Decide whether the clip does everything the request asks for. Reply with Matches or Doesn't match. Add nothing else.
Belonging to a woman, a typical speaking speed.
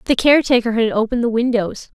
Matches